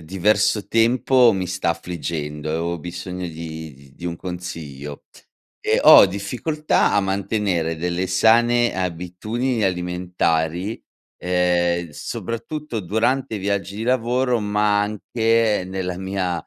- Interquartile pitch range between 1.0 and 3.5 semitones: No, average, 4.3 semitones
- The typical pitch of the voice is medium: No, very low, 95 Hz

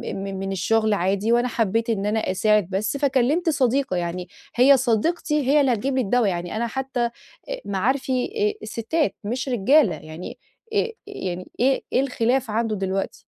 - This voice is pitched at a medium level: No, high, 230 Hz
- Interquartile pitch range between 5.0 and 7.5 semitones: Yes, average, 5.3 semitones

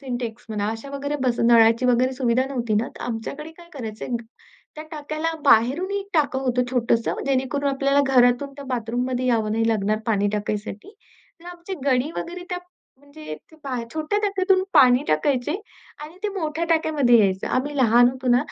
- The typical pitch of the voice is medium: No, very high, 255 Hz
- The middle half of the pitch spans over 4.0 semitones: Yes, average, 4.5 semitones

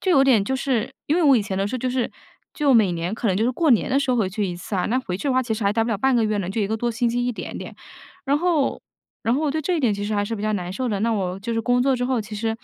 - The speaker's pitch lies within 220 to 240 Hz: Yes, high, 230 Hz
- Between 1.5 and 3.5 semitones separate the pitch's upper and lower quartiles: No, average, 4.1 semitones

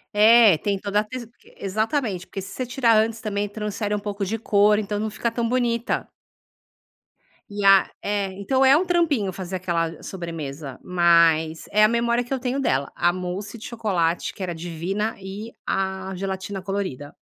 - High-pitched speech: Yes, high, 205 Hz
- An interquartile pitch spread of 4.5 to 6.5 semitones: No, average, 3.6 semitones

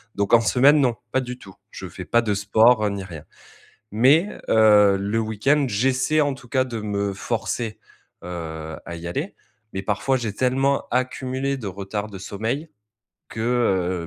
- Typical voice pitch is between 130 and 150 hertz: No, low, 110 Hz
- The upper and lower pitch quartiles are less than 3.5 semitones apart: No, average, 4.6 semitones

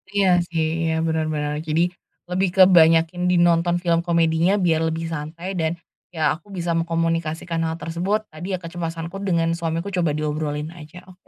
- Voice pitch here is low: No, medium, 165 Hz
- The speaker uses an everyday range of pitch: No, narrow, 1.5 semitones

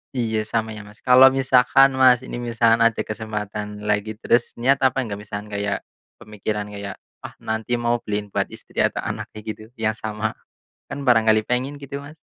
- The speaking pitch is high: No, low, 110 Hz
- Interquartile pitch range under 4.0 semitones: Yes, average, 2.9 semitones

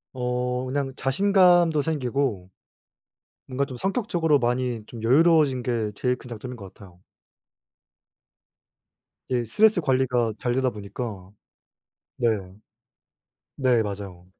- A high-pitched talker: No, low, 125 Hz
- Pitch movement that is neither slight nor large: Yes, average, 3.7 semitones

